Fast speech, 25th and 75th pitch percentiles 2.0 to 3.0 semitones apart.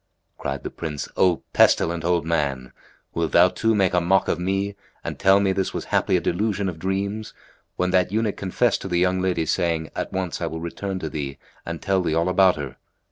Yes: fast, 215 wpm; average, 2.7 semitones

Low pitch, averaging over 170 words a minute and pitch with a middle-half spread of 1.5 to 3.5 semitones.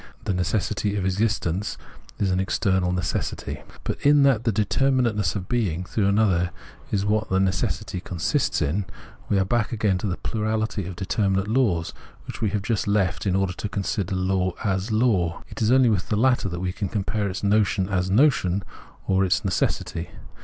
Yes: low, 100 Hz; average, 190 wpm; average, 2.8 semitones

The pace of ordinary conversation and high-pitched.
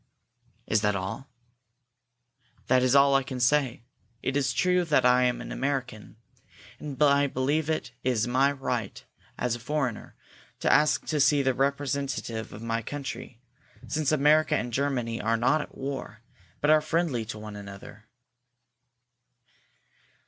No: average, 150 wpm; low, 130 Hz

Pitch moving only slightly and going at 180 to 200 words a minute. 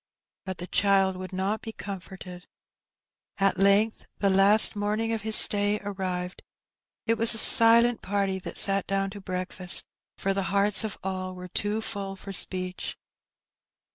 No: narrow, 1.8 semitones; average, 155 wpm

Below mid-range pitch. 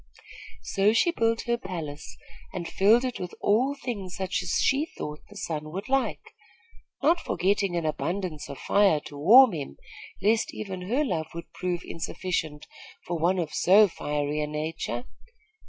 No: medium, 185 Hz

